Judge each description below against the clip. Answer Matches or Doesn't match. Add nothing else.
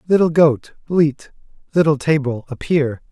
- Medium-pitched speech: Matches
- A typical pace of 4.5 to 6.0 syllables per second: Doesn't match